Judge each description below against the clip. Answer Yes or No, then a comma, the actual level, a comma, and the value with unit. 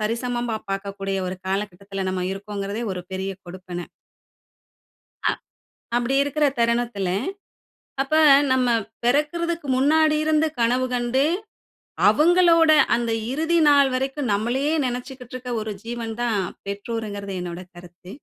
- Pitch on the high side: Yes, high, 235 Hz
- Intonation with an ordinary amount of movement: No, wide, 5.7 semitones